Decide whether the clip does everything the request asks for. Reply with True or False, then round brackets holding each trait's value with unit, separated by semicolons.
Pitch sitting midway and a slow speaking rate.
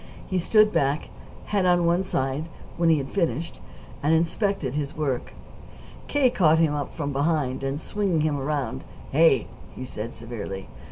False (155 Hz; 160 wpm)